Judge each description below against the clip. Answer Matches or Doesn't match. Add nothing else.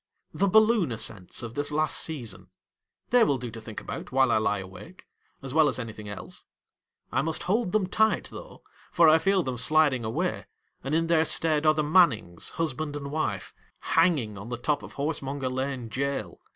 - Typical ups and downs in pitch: Doesn't match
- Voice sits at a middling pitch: Matches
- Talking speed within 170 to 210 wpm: Matches